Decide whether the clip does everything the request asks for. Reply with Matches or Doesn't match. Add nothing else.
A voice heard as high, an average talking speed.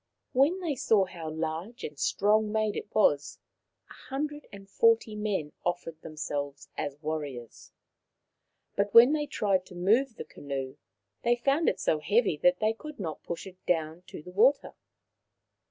Matches